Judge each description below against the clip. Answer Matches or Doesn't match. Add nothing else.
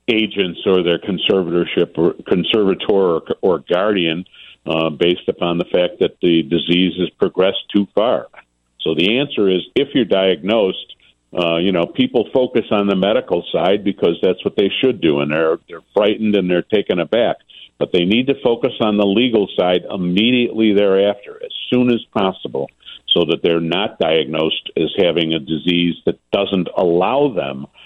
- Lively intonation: Doesn't match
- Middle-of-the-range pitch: Doesn't match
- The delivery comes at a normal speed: Matches